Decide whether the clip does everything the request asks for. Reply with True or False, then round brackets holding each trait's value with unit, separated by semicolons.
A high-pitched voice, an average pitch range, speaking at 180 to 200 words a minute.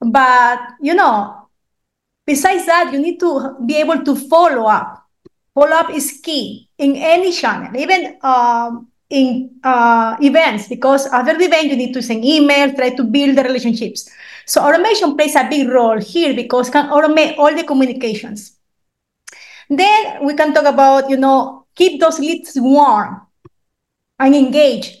False (275 Hz; 3.8 semitones; 160 wpm)